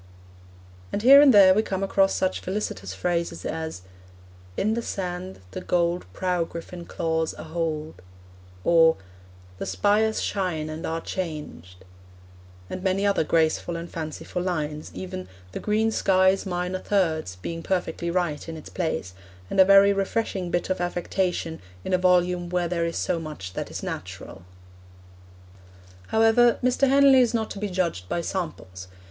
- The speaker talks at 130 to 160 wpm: Yes, average, 155 wpm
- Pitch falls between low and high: Yes, medium, 180 Hz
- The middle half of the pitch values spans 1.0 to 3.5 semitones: Yes, average, 3.2 semitones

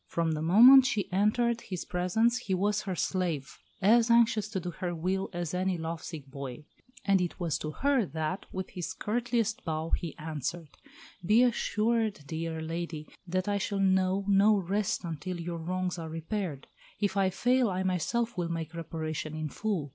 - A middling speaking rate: Yes, average, 175 wpm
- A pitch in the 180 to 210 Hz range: Yes, medium, 185 Hz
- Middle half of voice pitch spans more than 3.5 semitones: Yes, average, 4.3 semitones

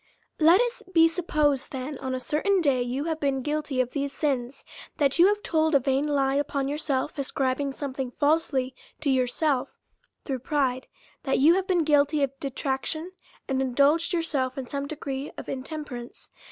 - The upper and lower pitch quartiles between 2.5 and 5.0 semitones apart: Yes, average, 2.9 semitones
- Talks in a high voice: Yes, very high, 280 Hz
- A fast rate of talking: No, average, 180 wpm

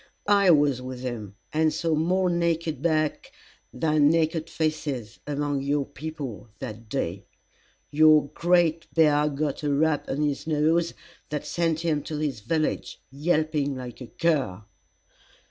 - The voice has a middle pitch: Yes, medium, 150 Hz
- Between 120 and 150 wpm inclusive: Yes, average, 140 wpm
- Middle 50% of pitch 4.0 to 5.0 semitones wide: No, average, 2.7 semitones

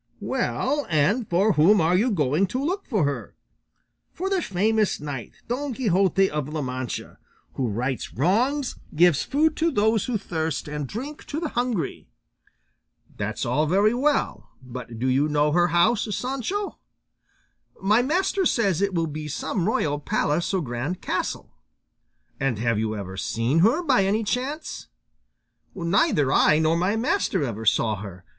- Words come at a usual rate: Yes, average, 155 wpm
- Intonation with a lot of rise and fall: Yes, wide, 8.8 semitones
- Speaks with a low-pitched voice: No, medium, 180 Hz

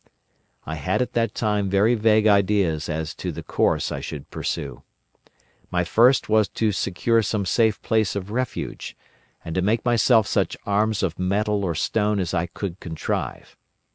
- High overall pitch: No, low, 105 Hz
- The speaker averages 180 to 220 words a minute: No, average, 170 wpm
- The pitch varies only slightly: No, average, 3.3 semitones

